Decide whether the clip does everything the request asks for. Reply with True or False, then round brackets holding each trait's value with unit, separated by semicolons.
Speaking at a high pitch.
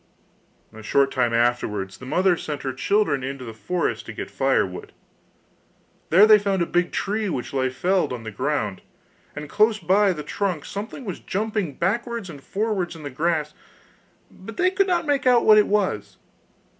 False (175 Hz)